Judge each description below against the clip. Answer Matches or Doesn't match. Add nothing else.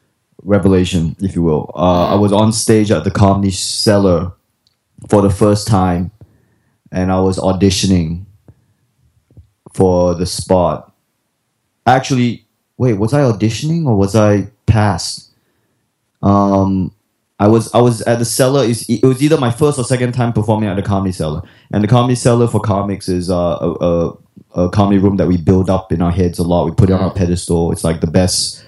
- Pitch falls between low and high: Doesn't match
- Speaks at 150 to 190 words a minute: Matches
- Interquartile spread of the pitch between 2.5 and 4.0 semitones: Matches